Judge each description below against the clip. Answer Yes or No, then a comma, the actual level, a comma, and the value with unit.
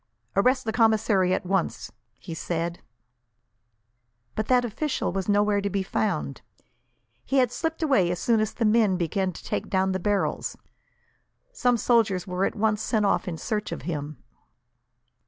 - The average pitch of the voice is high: Yes, high, 205 Hz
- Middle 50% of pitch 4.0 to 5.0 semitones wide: No, average, 3.6 semitones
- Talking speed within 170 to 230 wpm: No, average, 160 wpm